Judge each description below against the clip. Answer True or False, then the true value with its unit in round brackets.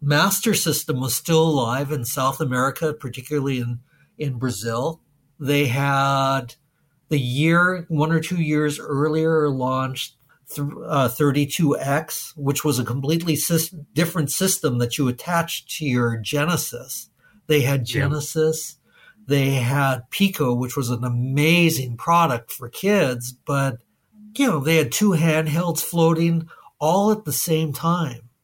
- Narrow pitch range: False (3.3 semitones)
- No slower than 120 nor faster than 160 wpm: True (135 wpm)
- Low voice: False (150 Hz)